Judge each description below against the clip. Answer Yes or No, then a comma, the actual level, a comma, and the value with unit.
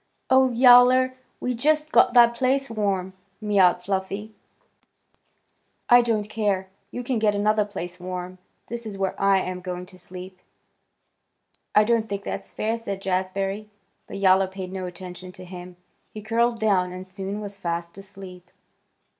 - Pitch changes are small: No, average, 3.5 semitones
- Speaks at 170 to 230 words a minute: No, average, 155 wpm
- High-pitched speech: Yes, high, 195 Hz